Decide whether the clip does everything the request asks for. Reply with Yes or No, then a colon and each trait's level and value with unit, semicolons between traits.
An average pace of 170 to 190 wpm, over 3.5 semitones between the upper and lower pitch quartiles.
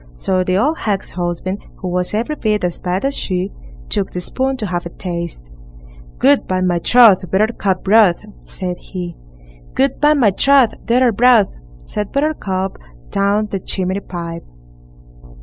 No: average, 155 wpm; average, 4.4 semitones